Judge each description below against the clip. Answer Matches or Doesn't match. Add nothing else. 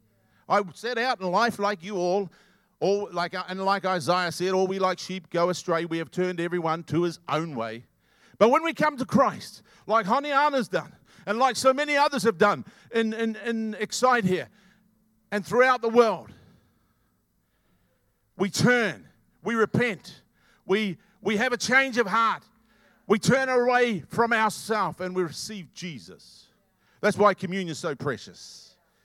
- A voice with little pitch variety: Doesn't match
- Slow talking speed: Doesn't match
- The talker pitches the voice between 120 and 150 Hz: Doesn't match